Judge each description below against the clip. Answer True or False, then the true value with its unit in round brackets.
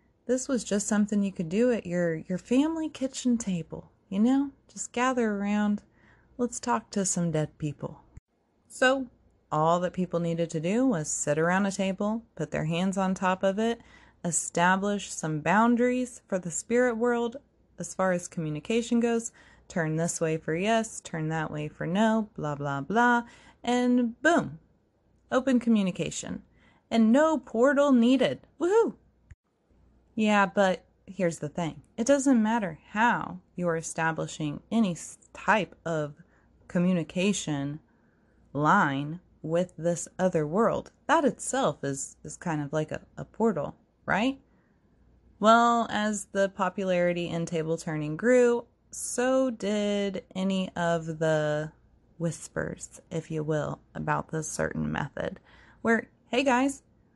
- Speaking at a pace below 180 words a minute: True (140 wpm)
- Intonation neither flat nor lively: False (6.3 semitones)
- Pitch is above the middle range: True (195 Hz)